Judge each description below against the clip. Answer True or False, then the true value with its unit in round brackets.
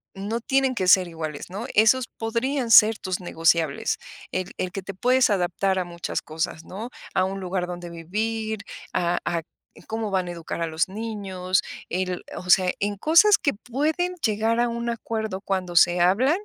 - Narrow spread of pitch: False (4.3 semitones)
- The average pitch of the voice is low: False (195 Hz)